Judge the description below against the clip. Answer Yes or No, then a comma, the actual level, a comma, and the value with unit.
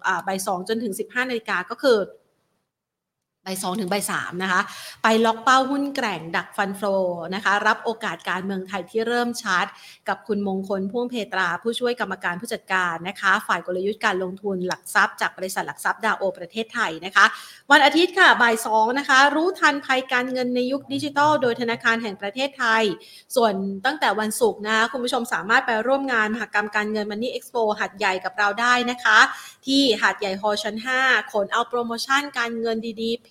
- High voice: Yes, high, 220 Hz